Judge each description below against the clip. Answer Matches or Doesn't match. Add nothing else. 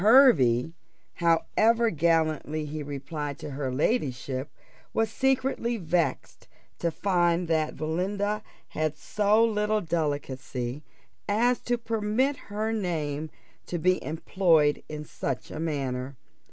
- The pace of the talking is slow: Matches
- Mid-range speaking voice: Matches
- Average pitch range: Doesn't match